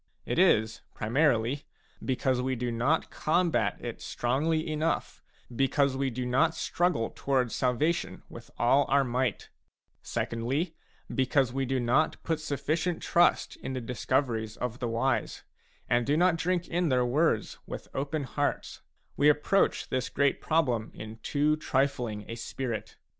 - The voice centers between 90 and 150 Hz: Yes, low, 135 Hz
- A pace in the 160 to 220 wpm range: No, average, 145 wpm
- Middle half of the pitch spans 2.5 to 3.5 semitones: No, average, 4.1 semitones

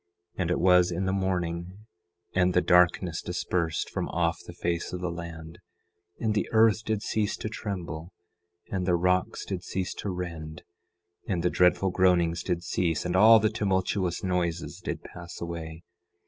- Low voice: Yes, very low, 90 Hz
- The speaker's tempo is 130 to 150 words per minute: No, average, 165 wpm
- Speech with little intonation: Yes, narrow, 1.8 semitones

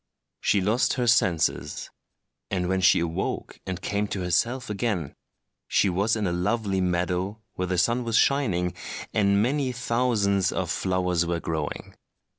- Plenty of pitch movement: No, average, 4.3 semitones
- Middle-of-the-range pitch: No, very low, 95 Hz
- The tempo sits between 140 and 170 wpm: Yes, average, 150 wpm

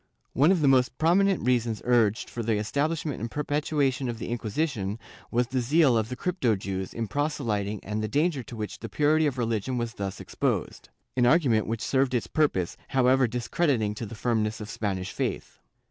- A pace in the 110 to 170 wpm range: No, average, 190 wpm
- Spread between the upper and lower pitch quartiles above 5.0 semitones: No, average, 4.7 semitones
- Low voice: Yes, low, 120 Hz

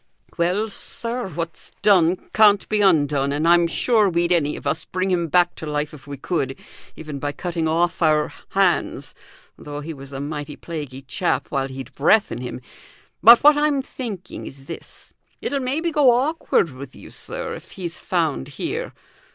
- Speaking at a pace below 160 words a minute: No, average, 175 wpm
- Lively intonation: Yes, wide, 5.7 semitones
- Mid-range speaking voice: Yes, medium, 170 Hz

